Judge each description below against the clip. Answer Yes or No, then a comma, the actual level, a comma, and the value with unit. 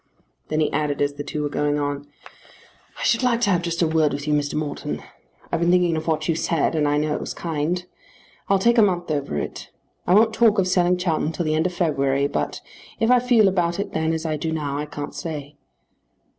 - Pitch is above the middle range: No, medium, 160 Hz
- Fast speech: Yes, fast, 240 wpm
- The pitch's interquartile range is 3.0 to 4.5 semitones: Yes, average, 3.4 semitones